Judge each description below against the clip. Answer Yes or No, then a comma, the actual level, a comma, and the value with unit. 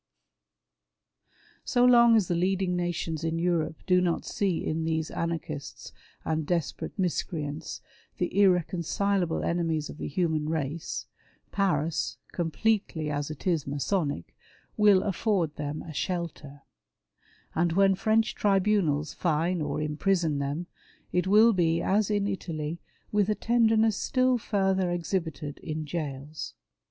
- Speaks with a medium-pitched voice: Yes, medium, 170 Hz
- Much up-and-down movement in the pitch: No, average, 3.9 semitones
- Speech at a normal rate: No, slow, 125 wpm